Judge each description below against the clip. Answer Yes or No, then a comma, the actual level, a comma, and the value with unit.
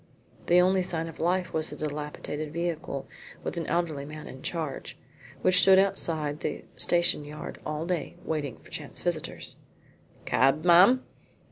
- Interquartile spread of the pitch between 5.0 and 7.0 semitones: No, average, 2.8 semitones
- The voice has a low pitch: No, medium, 160 Hz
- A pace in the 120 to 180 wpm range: Yes, average, 150 wpm